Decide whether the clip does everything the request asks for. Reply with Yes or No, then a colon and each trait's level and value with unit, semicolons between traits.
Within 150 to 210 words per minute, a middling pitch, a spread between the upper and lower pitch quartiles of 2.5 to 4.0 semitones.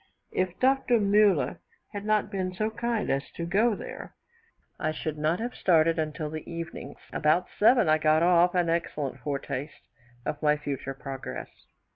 No: average, 160 wpm; medium, 170 Hz; average, 5.1 semitones